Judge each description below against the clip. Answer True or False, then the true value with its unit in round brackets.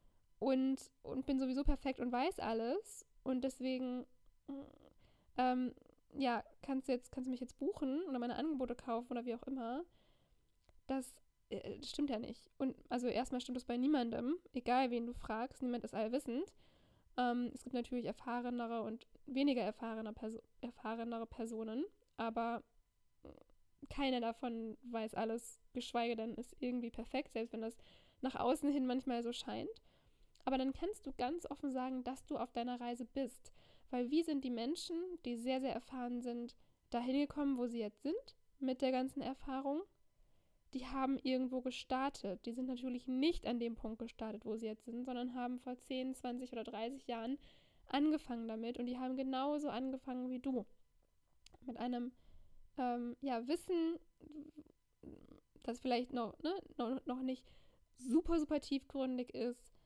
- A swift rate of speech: False (160 wpm)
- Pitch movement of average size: False (2.2 semitones)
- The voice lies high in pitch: True (255 Hz)